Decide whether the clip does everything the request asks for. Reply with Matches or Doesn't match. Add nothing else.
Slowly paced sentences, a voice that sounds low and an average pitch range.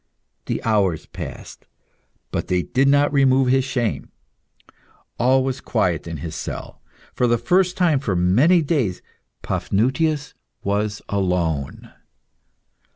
Doesn't match